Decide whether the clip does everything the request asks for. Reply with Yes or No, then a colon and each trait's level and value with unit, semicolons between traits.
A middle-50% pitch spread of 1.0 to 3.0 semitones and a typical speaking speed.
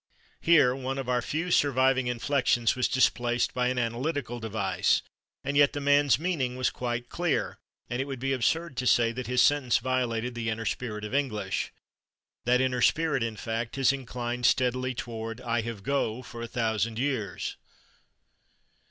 Yes: narrow, 2.5 semitones; average, 170 wpm